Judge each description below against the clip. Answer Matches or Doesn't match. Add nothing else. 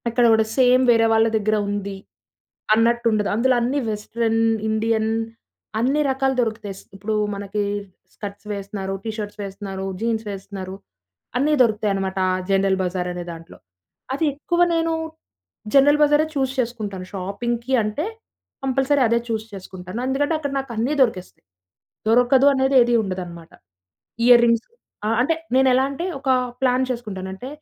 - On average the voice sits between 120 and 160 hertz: Doesn't match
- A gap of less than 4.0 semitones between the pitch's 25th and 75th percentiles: Doesn't match